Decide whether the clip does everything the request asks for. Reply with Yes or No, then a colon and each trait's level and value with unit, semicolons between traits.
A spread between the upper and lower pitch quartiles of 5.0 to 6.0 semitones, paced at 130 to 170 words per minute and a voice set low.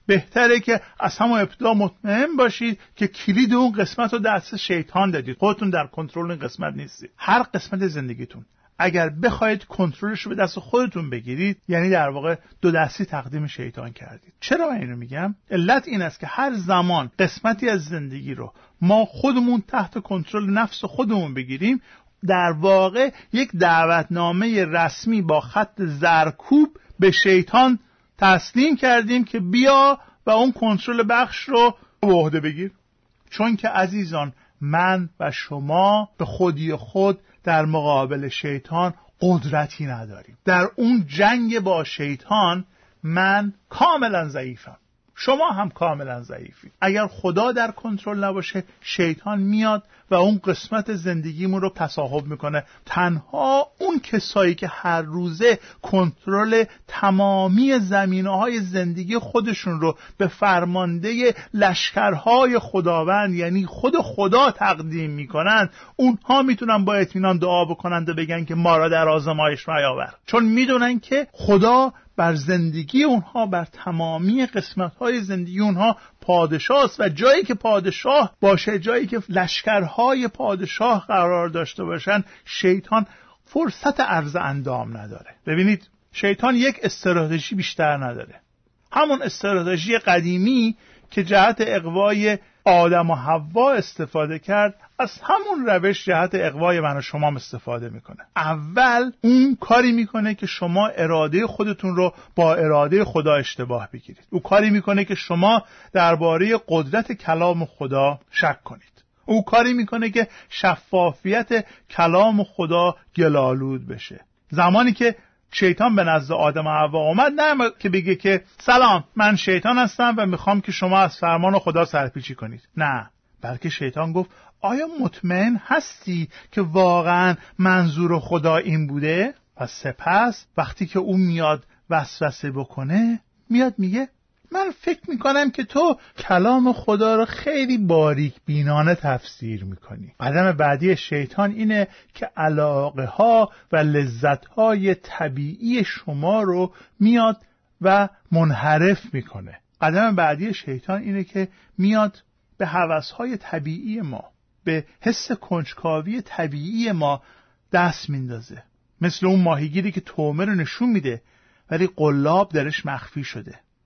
No: average, 5.3 semitones; average, 135 wpm; high, 190 Hz